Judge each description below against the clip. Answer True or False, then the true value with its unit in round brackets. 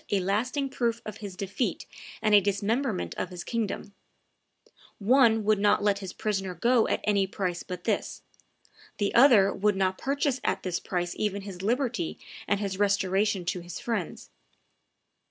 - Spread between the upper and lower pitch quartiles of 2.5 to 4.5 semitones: True (2.9 semitones)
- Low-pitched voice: False (205 Hz)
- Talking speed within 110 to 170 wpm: True (160 wpm)